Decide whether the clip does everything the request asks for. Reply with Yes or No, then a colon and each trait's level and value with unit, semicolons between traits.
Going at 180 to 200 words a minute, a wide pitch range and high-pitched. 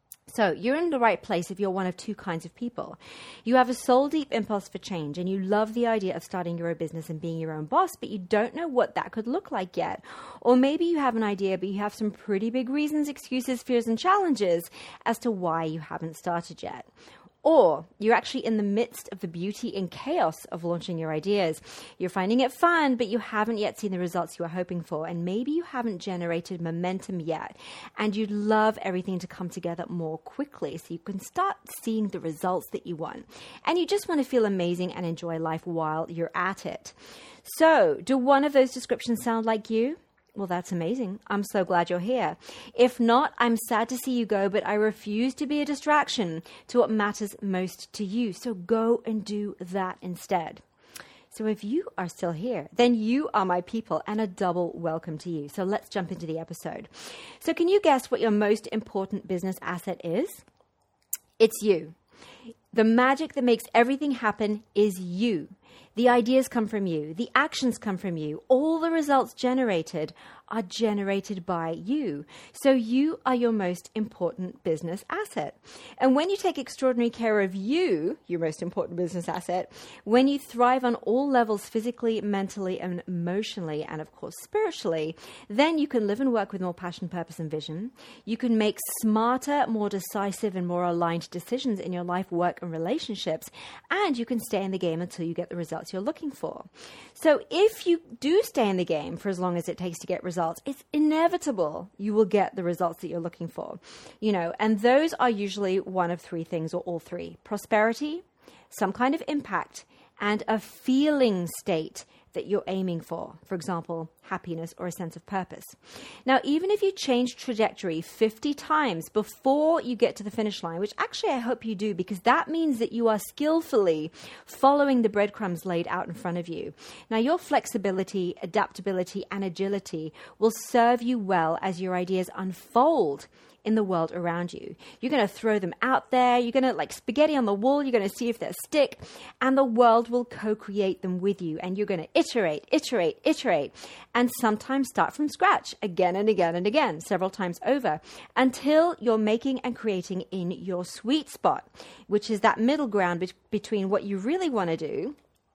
Yes: average, 195 wpm; wide, 5.7 semitones; high, 210 Hz